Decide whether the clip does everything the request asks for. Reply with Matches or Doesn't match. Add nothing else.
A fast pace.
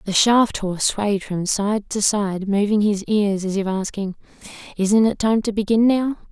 Doesn't match